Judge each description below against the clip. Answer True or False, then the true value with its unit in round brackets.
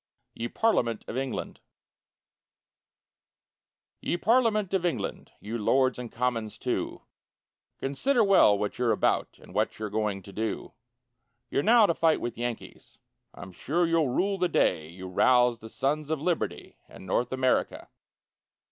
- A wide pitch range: True (7.6 semitones)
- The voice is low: True (125 Hz)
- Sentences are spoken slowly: False (145 wpm)